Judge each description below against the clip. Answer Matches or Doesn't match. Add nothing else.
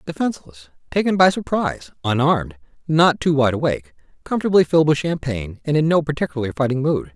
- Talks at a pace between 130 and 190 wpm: Matches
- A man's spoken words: Matches